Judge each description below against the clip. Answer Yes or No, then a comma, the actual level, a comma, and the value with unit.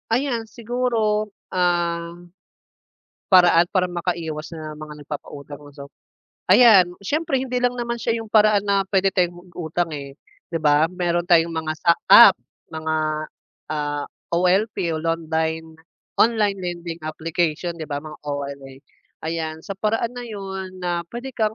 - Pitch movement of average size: Yes, average, 4.9 semitones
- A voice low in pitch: No, medium, 175 Hz